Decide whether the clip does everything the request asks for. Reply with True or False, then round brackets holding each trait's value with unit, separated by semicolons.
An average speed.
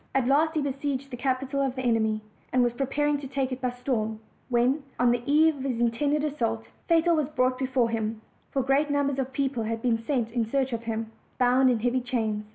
False (220 wpm)